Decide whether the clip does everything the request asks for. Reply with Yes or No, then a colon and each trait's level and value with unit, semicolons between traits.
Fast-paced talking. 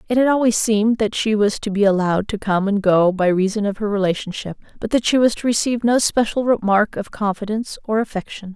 Yes: fast, 225 wpm